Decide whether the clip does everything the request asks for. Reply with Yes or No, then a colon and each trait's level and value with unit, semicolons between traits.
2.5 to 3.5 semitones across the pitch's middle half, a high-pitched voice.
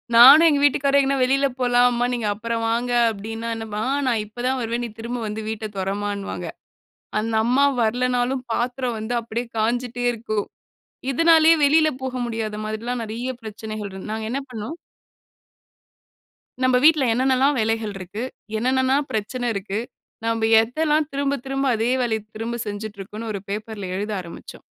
Yes: average, 3.1 semitones; high, 235 Hz